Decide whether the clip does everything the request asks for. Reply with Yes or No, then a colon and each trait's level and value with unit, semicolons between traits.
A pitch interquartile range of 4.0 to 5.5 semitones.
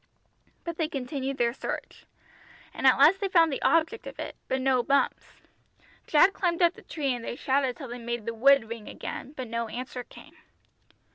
Yes: average, 4.5 semitones